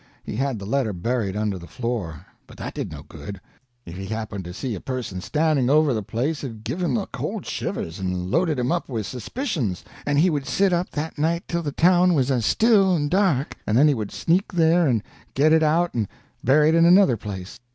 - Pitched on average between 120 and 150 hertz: Yes, low, 135 Hz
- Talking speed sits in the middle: No, fast, 225 wpm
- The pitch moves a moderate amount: No, wide, 7.3 semitones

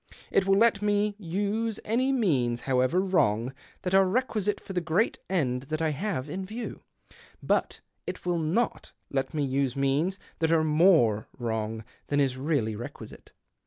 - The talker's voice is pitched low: No, medium, 165 Hz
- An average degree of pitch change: No, wide, 7.0 semitones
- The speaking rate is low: No, average, 160 wpm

